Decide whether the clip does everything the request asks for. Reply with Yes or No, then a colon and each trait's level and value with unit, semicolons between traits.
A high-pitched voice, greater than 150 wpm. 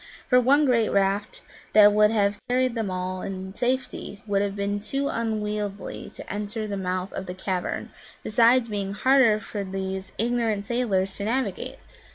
Yes: high, 210 Hz; average, 165 wpm